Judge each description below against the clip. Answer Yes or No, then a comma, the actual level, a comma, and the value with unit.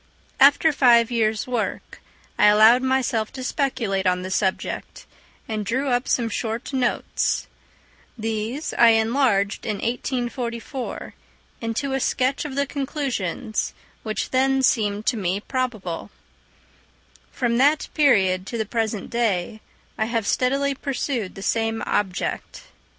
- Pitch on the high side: Yes, high, 235 Hz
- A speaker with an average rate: No, slow, 130 wpm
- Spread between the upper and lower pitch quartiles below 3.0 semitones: No, average, 3.5 semitones